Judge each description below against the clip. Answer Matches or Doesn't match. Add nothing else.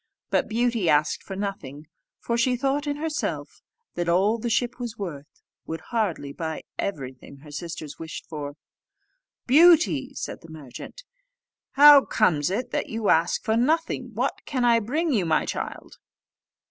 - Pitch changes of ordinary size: Doesn't match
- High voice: Matches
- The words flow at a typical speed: Matches